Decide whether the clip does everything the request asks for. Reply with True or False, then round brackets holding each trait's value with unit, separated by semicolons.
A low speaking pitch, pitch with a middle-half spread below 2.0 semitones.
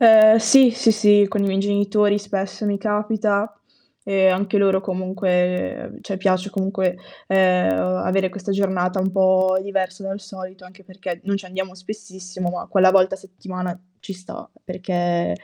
False (190 Hz; 1.5 semitones)